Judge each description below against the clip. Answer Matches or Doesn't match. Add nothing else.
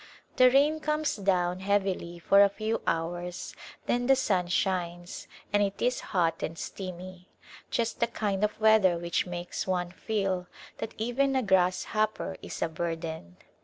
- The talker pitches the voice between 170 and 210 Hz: Matches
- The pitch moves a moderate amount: Matches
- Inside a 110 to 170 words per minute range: Matches